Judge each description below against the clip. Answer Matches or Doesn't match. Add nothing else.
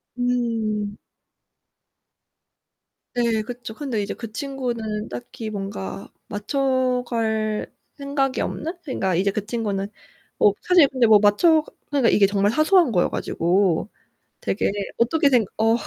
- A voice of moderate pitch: Doesn't match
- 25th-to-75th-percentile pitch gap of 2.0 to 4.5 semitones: Matches